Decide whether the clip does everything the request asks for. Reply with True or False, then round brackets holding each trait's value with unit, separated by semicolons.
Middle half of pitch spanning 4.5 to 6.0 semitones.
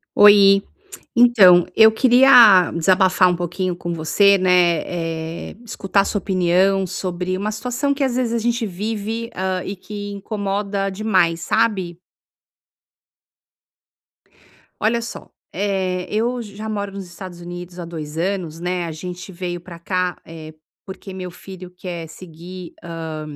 False (2.8 semitones)